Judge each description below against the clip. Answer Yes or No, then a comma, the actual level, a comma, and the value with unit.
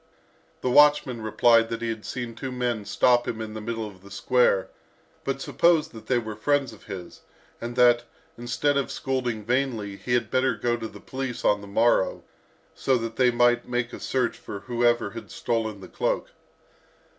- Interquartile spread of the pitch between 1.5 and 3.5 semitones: Yes, narrow, 2.4 semitones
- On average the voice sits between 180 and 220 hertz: No, low, 120 Hz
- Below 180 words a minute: No, average, 190 wpm